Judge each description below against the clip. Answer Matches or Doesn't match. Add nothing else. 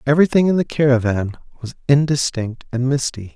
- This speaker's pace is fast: Doesn't match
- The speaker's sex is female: Doesn't match